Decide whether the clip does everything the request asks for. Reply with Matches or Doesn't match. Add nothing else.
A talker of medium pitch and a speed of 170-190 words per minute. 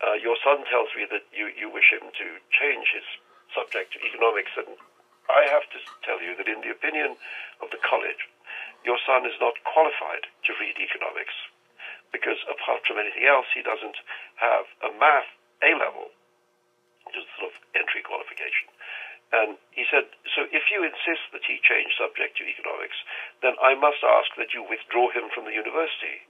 Doesn't match